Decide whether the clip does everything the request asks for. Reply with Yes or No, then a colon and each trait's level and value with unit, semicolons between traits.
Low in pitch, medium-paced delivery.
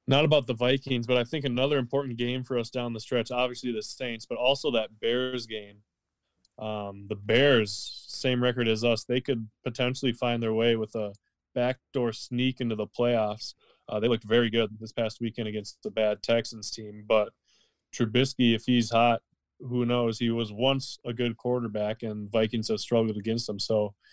Yes: low, 115 Hz; average, 190 wpm